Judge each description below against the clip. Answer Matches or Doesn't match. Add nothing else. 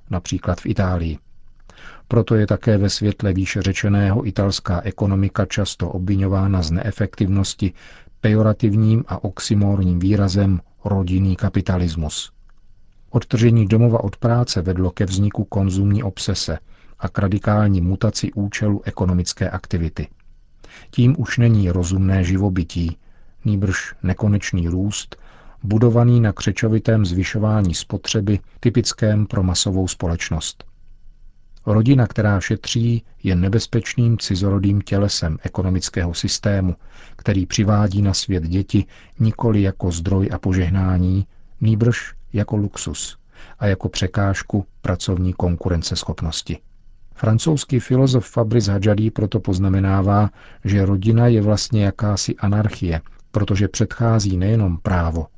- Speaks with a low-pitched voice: Matches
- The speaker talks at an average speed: Doesn't match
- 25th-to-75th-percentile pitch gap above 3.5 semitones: Doesn't match